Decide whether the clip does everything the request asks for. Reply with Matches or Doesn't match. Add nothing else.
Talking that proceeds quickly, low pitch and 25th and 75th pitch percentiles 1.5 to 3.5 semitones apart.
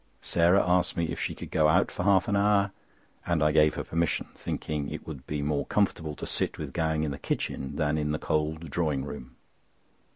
Matches